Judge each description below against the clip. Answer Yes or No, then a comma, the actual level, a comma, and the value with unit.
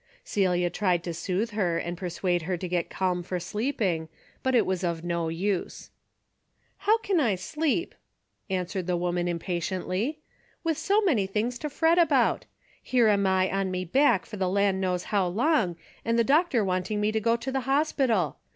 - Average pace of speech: Yes, average, 185 wpm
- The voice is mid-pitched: No, high, 195 Hz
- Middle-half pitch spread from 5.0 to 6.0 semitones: Yes, average, 5.3 semitones